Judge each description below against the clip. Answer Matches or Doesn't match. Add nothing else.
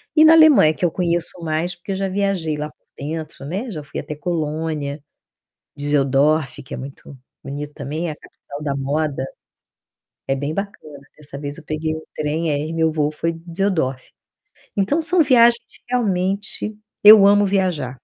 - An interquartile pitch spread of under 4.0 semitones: Doesn't match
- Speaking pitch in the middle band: Matches